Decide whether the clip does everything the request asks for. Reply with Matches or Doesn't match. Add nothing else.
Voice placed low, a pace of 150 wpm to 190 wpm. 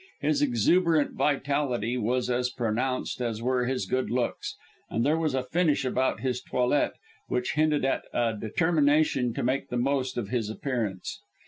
Matches